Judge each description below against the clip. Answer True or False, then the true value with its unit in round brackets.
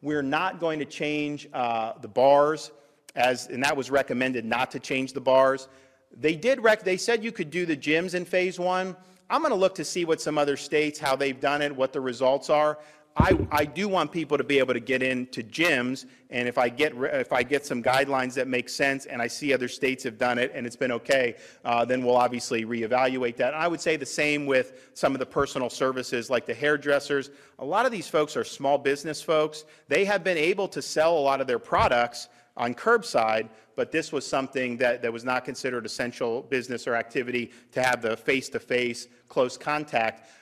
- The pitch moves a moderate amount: True (3.4 semitones)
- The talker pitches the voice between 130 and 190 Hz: True (135 Hz)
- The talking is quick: True (225 wpm)